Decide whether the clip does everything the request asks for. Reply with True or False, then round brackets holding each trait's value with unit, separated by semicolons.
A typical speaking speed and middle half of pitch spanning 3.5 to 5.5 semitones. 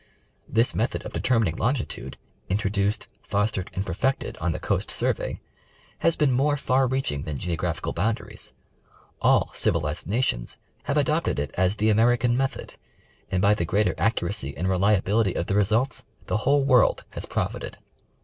True (155 wpm; 5.1 semitones)